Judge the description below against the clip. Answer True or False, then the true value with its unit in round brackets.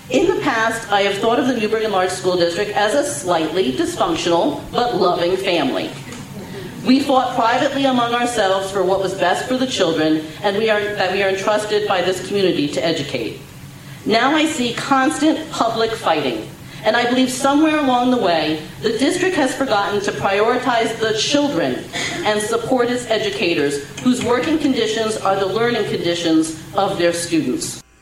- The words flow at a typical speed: True (170 wpm)